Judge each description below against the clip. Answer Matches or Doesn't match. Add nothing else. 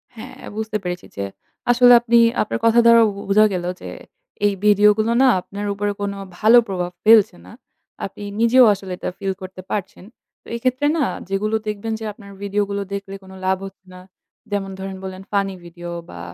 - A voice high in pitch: Matches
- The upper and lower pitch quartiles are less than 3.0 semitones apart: Matches